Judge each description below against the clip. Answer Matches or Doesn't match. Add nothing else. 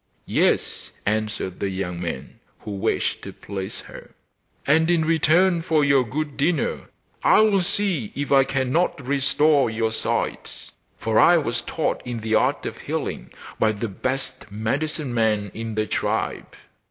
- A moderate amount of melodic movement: Doesn't match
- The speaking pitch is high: Doesn't match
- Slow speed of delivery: Doesn't match